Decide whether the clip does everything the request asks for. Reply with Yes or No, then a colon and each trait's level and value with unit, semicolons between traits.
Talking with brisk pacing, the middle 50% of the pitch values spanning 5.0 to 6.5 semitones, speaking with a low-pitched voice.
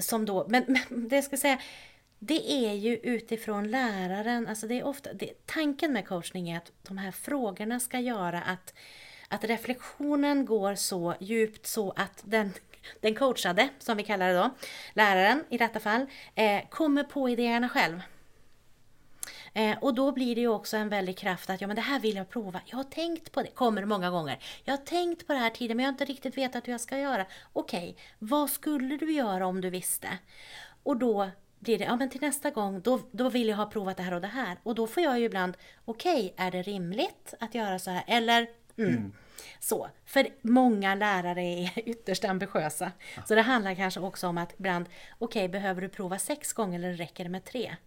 No: fast, 210 wpm; average, 5.3 semitones; high, 220 Hz